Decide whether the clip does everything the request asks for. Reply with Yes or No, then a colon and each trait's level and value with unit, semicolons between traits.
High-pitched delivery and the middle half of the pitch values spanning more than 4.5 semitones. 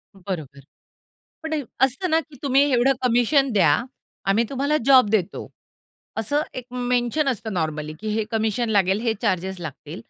Yes: high, 230 Hz; wide, 5.6 semitones